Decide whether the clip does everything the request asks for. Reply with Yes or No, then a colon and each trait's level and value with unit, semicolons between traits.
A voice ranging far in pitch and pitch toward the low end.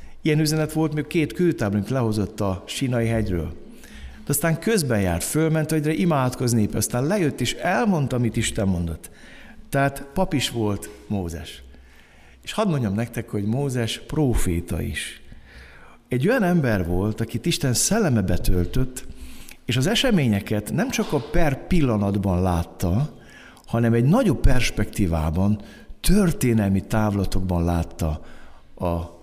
Yes: wide, 8.5 semitones; low, 115 Hz